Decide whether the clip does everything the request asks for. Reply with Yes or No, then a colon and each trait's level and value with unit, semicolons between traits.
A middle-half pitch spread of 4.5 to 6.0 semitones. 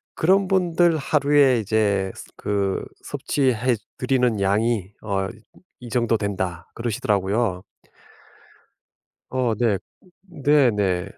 Yes: average, 5.2 semitones